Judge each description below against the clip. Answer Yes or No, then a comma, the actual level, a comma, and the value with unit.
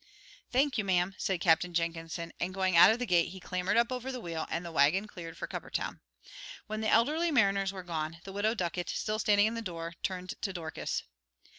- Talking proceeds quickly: Yes, fast, 210 wpm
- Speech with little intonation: No, average, 4.2 semitones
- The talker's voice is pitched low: No, medium, 185 Hz